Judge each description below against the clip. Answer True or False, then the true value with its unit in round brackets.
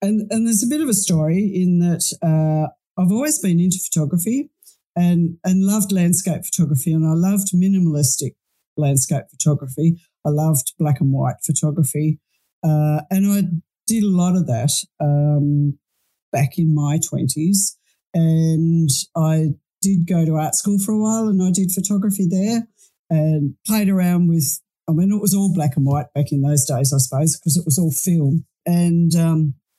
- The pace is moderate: True (175 wpm)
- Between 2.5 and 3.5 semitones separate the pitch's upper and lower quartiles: False (3.9 semitones)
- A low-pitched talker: False (165 Hz)